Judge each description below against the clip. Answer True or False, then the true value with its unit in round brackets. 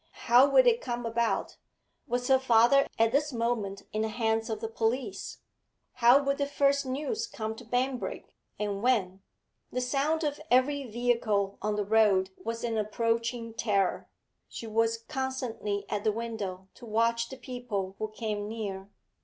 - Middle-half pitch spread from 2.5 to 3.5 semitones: True (3.1 semitones)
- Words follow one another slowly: False (160 wpm)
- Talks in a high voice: True (230 Hz)